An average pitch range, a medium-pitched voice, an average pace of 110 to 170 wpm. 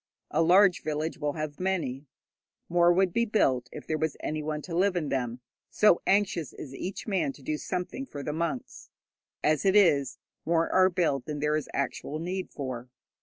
No: average, 4.1 semitones; medium, 160 Hz; average, 185 wpm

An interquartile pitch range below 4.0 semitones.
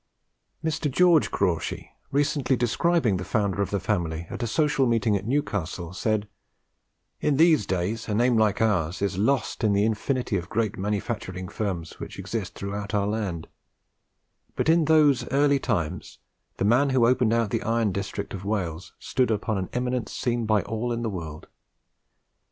No: average, 4.3 semitones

